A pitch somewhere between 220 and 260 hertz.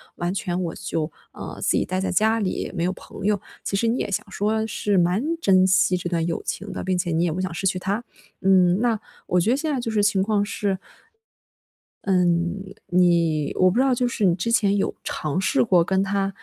No: high, 190 Hz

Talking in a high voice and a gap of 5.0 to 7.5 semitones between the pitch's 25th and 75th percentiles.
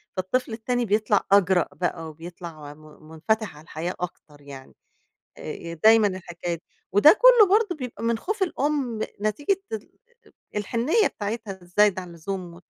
Yes: high, 200 Hz; wide, 5.5 semitones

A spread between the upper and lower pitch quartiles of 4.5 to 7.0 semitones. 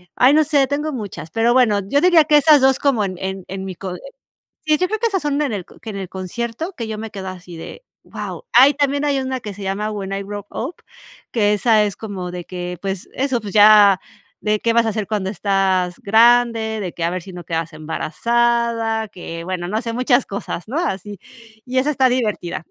Yes: average, 5.1 semitones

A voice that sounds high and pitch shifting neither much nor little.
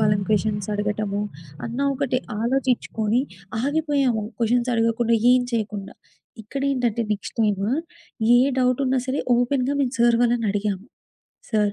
Yes: high, 235 Hz; average, 3.2 semitones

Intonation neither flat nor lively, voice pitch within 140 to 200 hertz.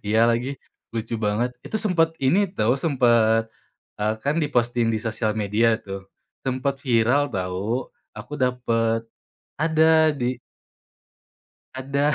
No: average, 3.9 semitones; low, 120 Hz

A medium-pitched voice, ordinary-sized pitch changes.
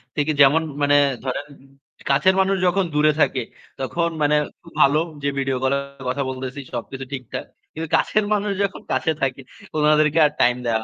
Yes: medium, 145 Hz; average, 3.5 semitones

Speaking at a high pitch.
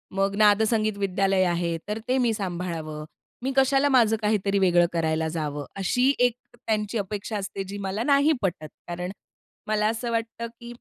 Yes: high, 205 Hz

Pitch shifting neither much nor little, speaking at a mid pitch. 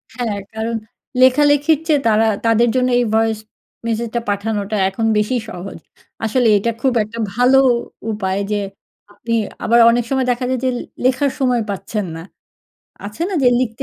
No: average, 3.1 semitones; high, 230 Hz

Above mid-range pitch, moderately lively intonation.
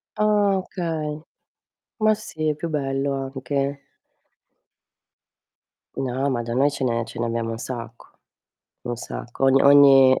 No: low, 135 Hz; average, 3.6 semitones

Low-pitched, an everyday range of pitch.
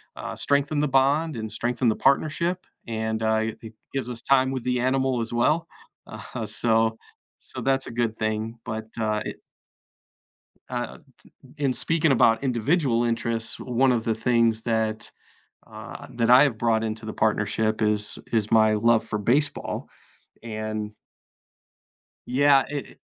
Yes: low, 115 Hz; average, 3.2 semitones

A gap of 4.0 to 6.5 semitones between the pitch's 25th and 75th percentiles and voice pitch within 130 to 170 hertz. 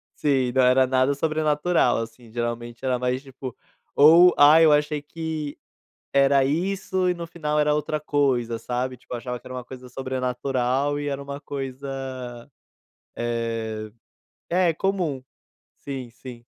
No: average, 3.1 semitones; low, 135 Hz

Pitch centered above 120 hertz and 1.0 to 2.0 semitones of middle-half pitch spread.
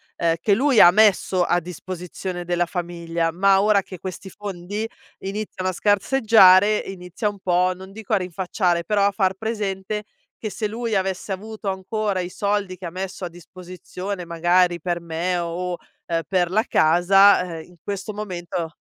No: medium, 185 Hz; narrow, 2.5 semitones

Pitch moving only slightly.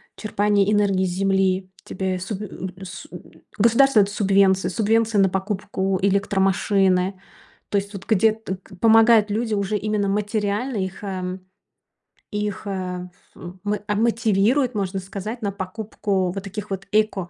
Yes: narrow, 1.9 semitones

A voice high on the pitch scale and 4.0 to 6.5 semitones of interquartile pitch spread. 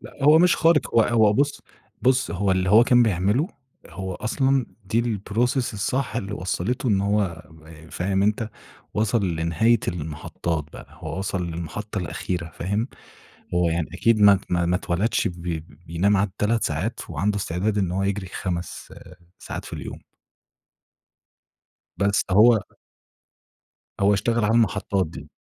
No: low, 100 Hz; average, 4.3 semitones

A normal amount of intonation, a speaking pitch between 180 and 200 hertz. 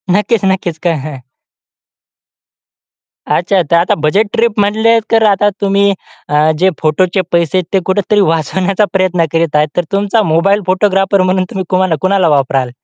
Yes: average, 3.3 semitones; medium, 185 Hz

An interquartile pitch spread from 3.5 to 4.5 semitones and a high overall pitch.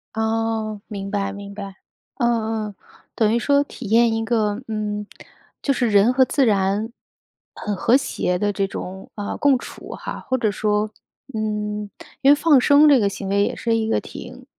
No: narrow, 2.6 semitones; high, 215 Hz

